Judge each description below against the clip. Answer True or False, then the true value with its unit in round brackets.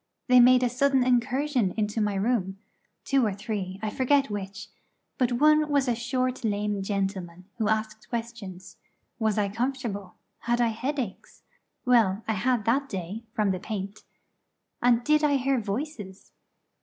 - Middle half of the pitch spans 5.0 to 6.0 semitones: False (4.1 semitones)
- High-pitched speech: True (225 Hz)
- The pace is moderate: True (155 wpm)